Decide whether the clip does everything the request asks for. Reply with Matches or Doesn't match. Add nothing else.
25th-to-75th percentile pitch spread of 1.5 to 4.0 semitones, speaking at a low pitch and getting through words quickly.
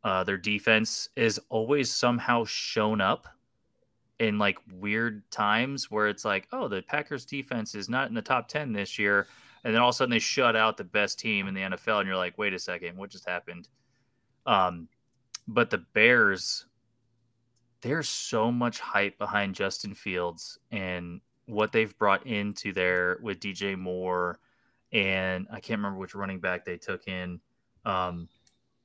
Doesn't match